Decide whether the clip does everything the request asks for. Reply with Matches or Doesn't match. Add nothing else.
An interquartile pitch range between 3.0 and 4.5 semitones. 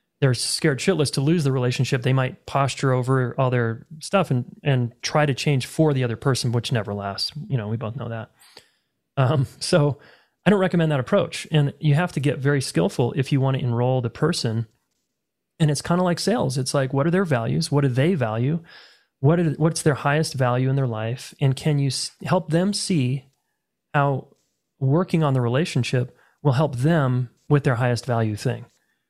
Matches